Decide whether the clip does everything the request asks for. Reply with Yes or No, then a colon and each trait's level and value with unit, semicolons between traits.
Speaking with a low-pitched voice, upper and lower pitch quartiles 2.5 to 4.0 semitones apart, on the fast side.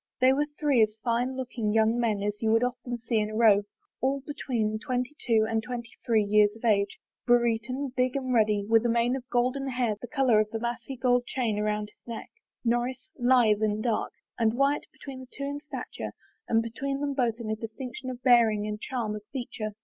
No: high, 235 Hz; average, 2.8 semitones; fast, 210 wpm